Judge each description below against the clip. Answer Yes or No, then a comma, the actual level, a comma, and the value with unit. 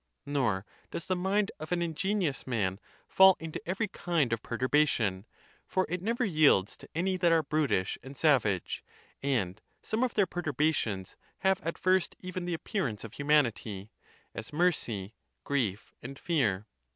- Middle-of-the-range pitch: Yes, medium, 150 Hz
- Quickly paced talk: No, average, 155 wpm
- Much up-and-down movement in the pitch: Yes, wide, 7.9 semitones